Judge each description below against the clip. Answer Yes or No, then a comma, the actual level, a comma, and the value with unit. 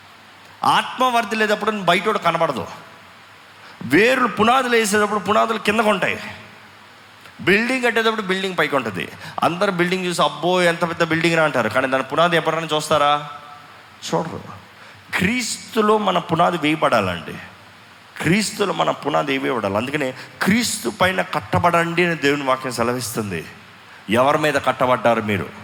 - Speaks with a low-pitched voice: No, medium, 170 Hz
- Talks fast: No, average, 115 wpm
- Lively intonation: Yes, wide, 6.5 semitones